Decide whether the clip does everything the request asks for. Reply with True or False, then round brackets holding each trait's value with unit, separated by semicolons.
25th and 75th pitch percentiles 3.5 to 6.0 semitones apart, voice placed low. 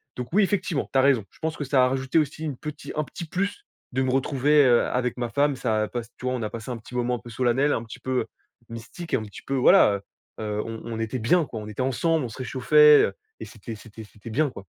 True (4.3 semitones; 125 Hz)